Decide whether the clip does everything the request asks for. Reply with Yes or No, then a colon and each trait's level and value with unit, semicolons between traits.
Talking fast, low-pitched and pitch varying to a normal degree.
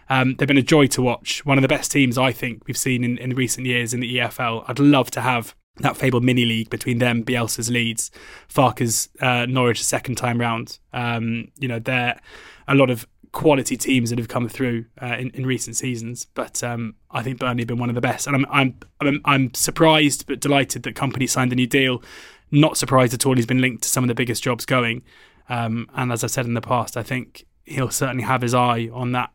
No: fast, 235 wpm; low, 125 Hz; narrow, 1.6 semitones